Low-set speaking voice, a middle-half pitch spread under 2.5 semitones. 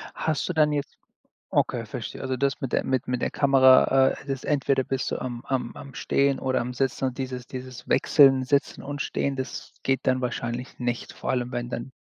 Yes: low, 130 Hz; narrow, 1.5 semitones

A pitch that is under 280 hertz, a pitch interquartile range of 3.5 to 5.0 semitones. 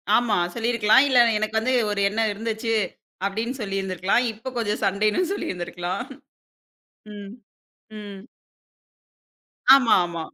No: high, 215 Hz; average, 3.0 semitones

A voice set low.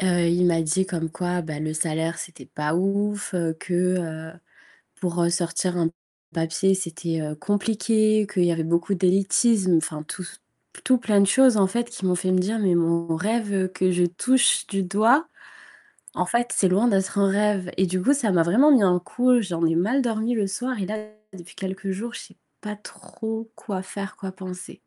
No: high, 190 Hz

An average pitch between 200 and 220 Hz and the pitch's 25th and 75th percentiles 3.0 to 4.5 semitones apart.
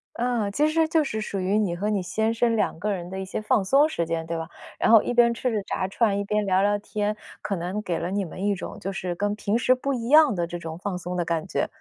Yes: high, 205 Hz; average, 4.0 semitones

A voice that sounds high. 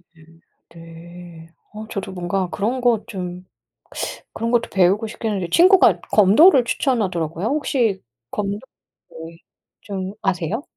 Yes: high, 195 Hz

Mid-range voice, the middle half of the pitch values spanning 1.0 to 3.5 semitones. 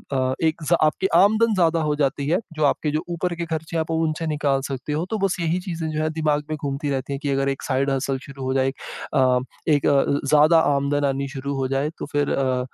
Yes: medium, 145 Hz; average, 2.8 semitones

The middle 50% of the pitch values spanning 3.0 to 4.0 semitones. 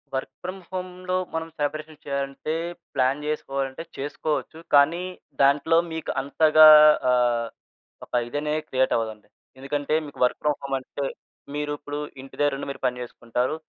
No: narrow, 2.6 semitones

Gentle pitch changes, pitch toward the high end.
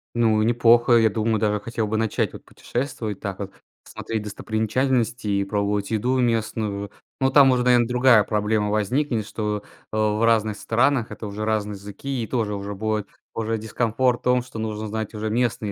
No: narrow, 2.2 semitones; low, 110 Hz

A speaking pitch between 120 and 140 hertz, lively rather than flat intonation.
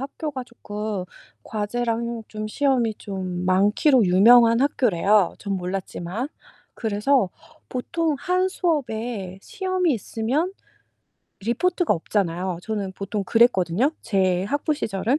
No: high, 225 Hz; wide, 5.8 semitones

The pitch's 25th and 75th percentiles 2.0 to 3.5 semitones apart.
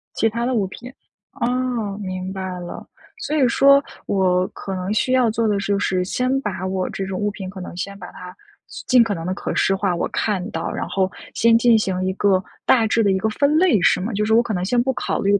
No: average, 4.0 semitones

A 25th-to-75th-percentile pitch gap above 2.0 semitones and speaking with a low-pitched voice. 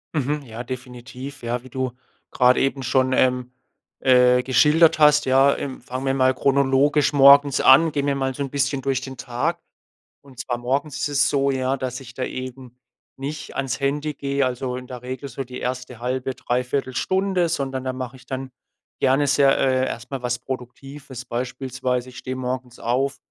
No: narrow, 1.6 semitones; low, 130 Hz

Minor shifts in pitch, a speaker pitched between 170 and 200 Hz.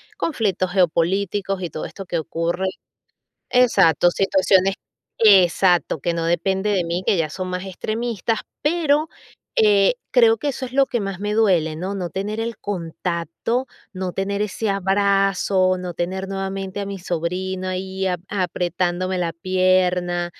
Yes: narrow, 2.2 semitones; high, 190 Hz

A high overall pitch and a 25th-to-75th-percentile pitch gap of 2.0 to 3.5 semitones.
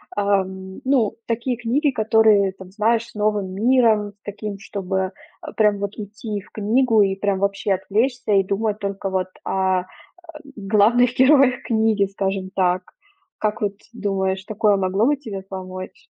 Yes: high, 205 Hz; narrow, 2.5 semitones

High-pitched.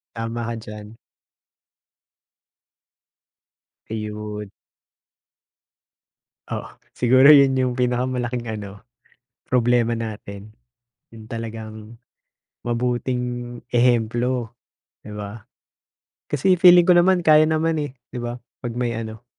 No: low, 120 Hz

